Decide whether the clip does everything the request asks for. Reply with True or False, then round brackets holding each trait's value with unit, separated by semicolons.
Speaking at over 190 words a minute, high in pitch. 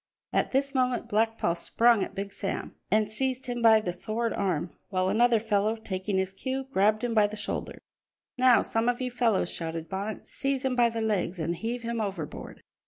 True (200 wpm; 220 Hz)